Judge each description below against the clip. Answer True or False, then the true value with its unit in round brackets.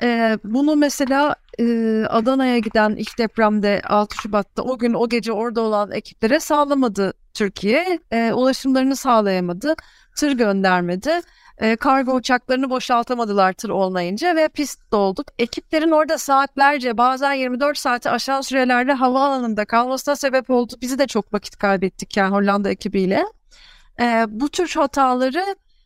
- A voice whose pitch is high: True (245 Hz)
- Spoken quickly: False (130 wpm)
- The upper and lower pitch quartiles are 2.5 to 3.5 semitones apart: False (4.5 semitones)